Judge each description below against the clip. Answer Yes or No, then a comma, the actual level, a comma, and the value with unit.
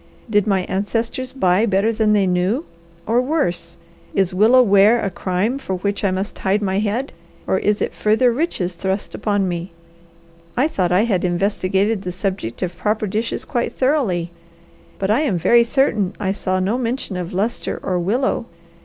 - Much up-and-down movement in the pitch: No, average, 3.7 semitones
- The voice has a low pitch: No, high, 200 Hz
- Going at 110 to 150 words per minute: No, average, 175 wpm